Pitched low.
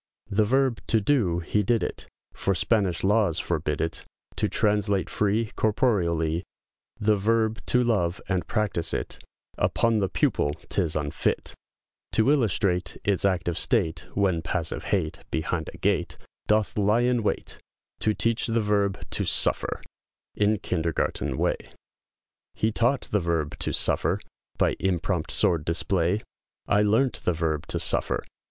Yes: low, 100 Hz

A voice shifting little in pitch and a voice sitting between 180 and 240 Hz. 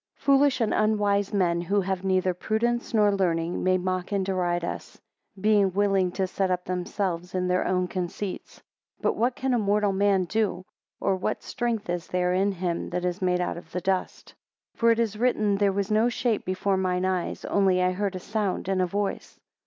Yes: narrow, 2.3 semitones; high, 190 Hz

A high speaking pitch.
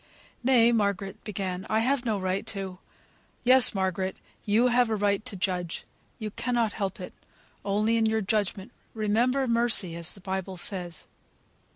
Yes: high, 205 Hz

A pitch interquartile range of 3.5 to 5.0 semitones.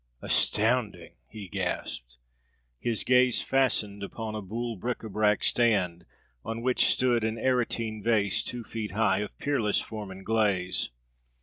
No: average, 2.8 semitones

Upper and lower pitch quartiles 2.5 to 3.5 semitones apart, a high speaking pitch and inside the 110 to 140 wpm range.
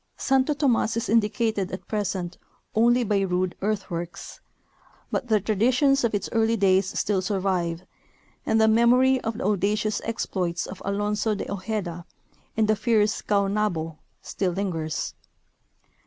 Yes: average, 3.2 semitones; high, 210 Hz; slow, 135 wpm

